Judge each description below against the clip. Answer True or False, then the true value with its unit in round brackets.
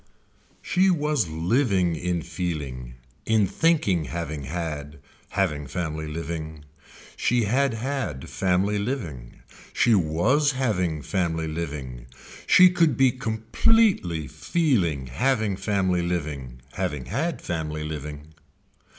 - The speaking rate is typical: False (105 wpm)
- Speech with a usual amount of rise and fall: False (7.4 semitones)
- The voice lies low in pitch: True (85 Hz)